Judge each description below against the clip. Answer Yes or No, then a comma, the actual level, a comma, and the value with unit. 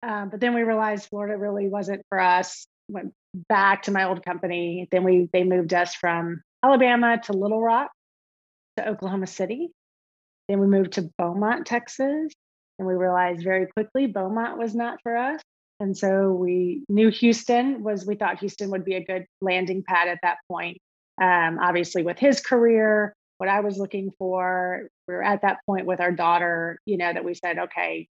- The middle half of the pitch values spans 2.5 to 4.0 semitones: Yes, average, 3.1 semitones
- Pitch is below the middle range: No, high, 195 Hz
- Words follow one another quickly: No, average, 185 wpm